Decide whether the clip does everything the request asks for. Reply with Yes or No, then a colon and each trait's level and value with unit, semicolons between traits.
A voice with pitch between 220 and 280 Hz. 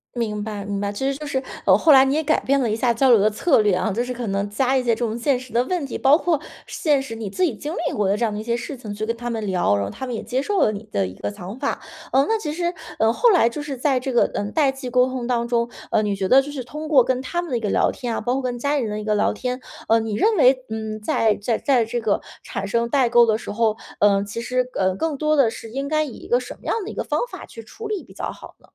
Yes: high, 240 Hz